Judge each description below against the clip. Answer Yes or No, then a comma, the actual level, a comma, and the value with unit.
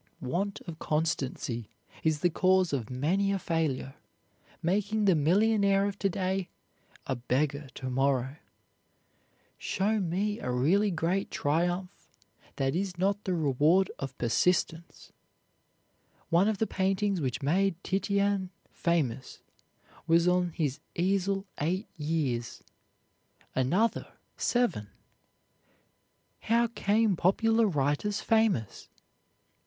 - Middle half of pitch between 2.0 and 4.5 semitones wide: No, wide, 5.4 semitones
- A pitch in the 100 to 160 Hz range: No, medium, 180 Hz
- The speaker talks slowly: Yes, slow, 110 wpm